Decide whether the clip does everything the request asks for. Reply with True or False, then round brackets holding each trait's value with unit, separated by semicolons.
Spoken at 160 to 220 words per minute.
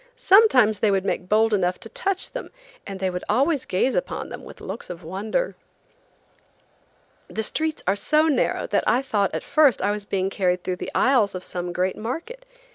True (195 wpm)